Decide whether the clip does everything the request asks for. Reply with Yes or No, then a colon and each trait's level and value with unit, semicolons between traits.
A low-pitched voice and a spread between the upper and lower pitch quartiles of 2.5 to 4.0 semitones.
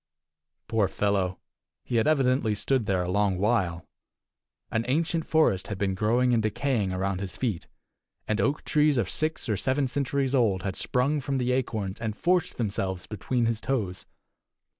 No: low, 115 Hz; wide, 5.5 semitones